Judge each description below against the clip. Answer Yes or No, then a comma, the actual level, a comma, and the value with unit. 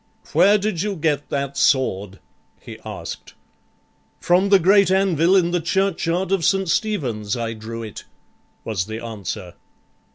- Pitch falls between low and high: Yes, medium, 165 Hz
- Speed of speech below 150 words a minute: Yes, average, 140 wpm